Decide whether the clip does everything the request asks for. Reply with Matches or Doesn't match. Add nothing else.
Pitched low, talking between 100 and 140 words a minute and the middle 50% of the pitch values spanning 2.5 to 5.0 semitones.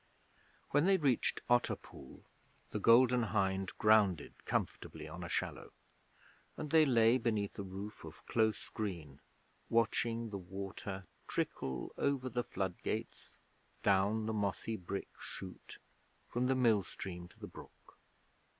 Matches